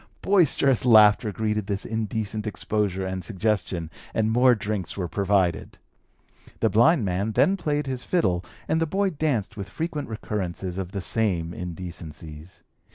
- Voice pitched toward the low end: Yes, low, 105 Hz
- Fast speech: No, average, 145 wpm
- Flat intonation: No, average, 4.8 semitones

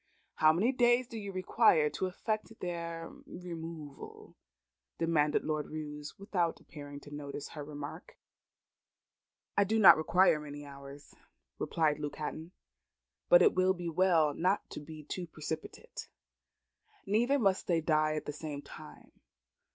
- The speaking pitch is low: No, medium, 165 Hz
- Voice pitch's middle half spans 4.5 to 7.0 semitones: No, average, 4.0 semitones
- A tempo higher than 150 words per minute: No, average, 140 wpm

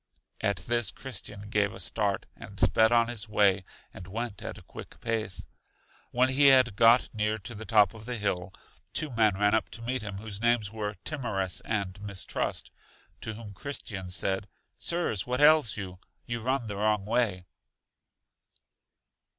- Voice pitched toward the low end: Yes, low, 110 Hz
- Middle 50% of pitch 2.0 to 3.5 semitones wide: Yes, average, 2.9 semitones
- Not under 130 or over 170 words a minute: Yes, average, 165 wpm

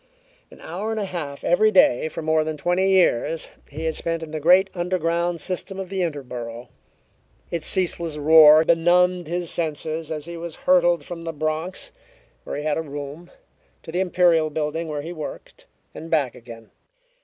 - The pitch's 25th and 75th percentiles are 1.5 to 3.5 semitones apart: Yes, narrow, 2.4 semitones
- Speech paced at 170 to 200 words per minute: Yes, average, 180 wpm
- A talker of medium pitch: Yes, medium, 165 Hz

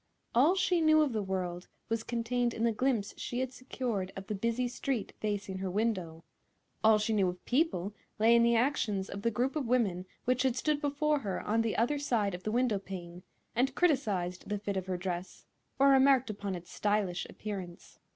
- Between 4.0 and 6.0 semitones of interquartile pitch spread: Yes, average, 4.8 semitones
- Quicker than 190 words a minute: Yes, average, 200 wpm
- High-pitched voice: Yes, high, 220 Hz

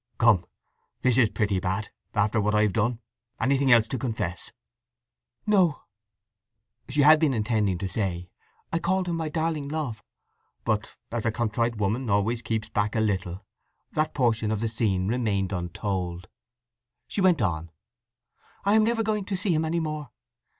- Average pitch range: No, wide, 6.9 semitones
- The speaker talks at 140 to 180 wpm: Yes, average, 155 wpm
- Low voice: Yes, low, 115 Hz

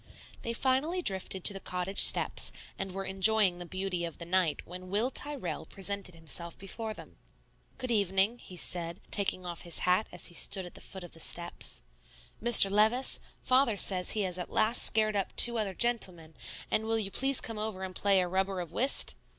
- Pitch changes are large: No, average, 3.5 semitones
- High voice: Yes, high, 195 Hz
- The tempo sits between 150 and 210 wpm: Yes, average, 200 wpm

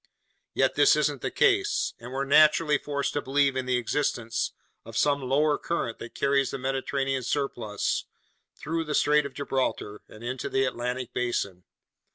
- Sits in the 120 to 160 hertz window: Yes, low, 135 Hz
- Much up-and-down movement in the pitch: No, average, 2.9 semitones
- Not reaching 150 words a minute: No, average, 165 wpm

